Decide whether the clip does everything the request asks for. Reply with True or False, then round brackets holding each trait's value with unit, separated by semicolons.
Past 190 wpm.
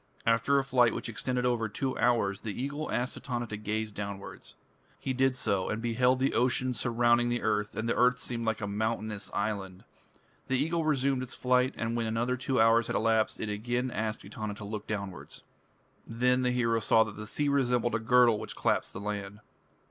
True (200 wpm)